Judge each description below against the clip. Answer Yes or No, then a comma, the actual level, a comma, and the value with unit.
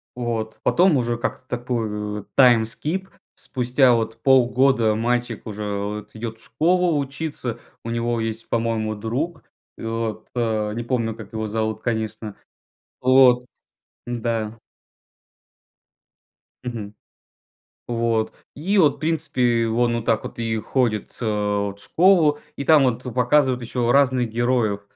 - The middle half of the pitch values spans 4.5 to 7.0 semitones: No, narrow, 2.6 semitones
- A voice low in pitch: Yes, low, 120 Hz